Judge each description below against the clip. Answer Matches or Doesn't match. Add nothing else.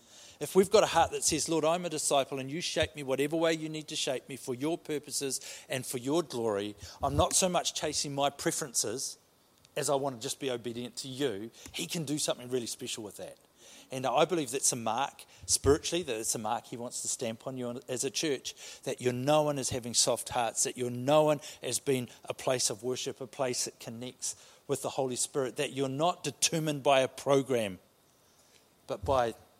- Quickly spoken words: Matches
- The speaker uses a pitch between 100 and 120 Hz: Doesn't match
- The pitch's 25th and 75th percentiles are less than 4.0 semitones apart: Matches